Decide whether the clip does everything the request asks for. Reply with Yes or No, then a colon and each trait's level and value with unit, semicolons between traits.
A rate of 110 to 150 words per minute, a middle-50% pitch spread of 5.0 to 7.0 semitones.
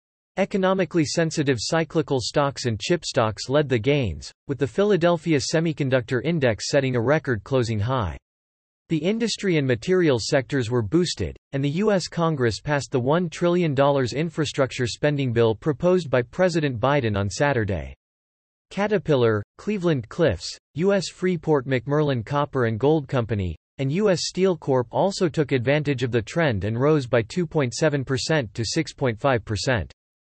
Yes: average, 140 wpm; average, 5.3 semitones